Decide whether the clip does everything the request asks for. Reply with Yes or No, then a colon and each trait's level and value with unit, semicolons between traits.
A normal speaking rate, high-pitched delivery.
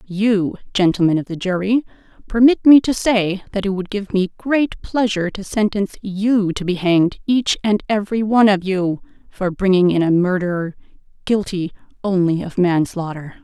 Yes: average, 165 wpm; high, 195 Hz